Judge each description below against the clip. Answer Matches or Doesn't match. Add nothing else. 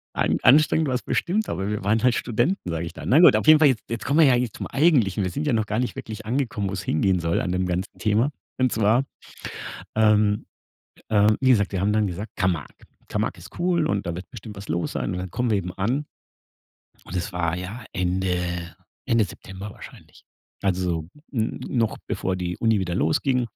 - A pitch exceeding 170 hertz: Doesn't match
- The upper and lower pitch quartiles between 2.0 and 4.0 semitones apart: Doesn't match